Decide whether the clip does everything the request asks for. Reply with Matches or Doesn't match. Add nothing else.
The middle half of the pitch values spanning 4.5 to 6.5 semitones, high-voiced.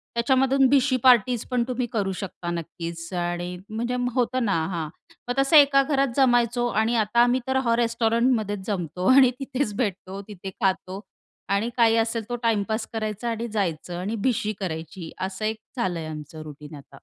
Matches